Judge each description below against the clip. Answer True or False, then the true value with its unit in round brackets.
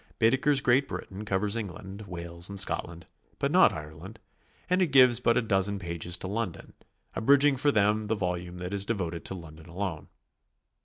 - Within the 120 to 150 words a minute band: False (170 wpm)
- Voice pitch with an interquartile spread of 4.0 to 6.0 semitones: True (4.8 semitones)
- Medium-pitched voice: False (100 Hz)